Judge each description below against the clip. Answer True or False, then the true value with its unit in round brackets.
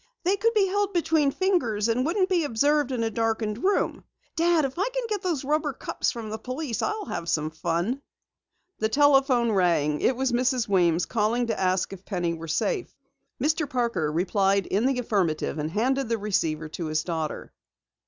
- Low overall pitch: False (235 Hz)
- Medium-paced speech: True (190 wpm)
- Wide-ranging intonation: True (8.0 semitones)